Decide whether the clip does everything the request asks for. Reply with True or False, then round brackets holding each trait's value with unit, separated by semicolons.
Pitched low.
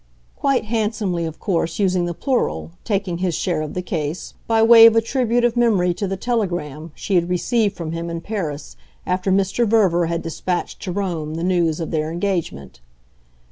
False (180 Hz)